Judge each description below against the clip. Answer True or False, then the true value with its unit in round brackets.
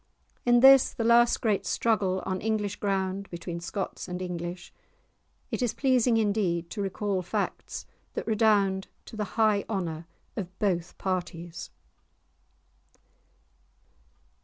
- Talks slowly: True (120 wpm)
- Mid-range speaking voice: False (195 Hz)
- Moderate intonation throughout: True (3.4 semitones)